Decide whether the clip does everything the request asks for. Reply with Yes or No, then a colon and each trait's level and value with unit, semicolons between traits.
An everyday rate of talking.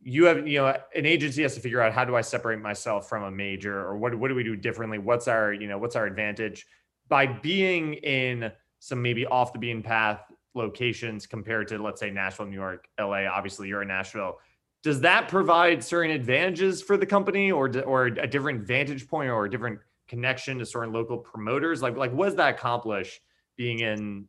No: fast, 210 wpm